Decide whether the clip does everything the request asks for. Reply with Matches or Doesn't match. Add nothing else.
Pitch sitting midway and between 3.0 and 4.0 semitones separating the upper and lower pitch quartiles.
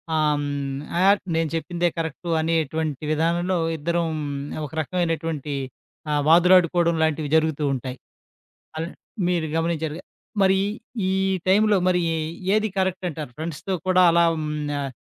Doesn't match